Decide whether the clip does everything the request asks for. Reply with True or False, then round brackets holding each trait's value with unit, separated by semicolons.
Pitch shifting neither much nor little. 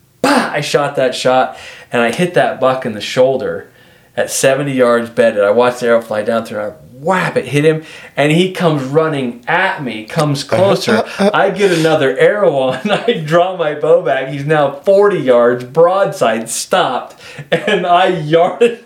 False (6.0 semitones)